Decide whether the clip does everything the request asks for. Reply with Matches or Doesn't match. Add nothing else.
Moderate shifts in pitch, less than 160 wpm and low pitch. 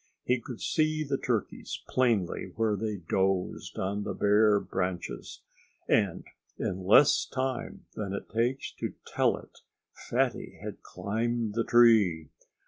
Matches